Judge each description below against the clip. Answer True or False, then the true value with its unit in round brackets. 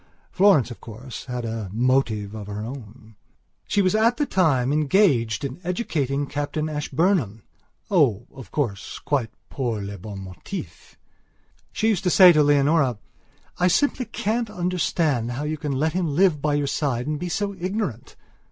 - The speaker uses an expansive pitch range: True (7.0 semitones)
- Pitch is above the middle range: False (145 Hz)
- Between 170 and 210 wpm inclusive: False (160 wpm)